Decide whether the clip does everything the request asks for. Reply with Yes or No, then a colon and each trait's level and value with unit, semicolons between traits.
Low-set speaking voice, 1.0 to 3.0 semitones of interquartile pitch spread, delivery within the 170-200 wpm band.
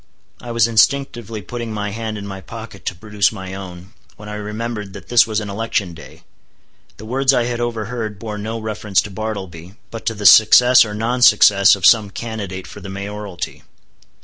Yes: low, 105 Hz; narrow, 2.5 semitones; average, 190 wpm